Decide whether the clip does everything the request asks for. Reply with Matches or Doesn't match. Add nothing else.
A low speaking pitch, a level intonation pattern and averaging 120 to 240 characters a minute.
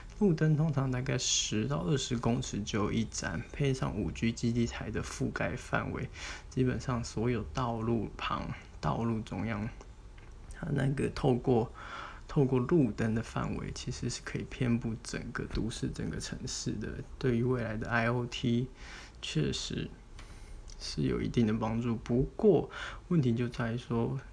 Matches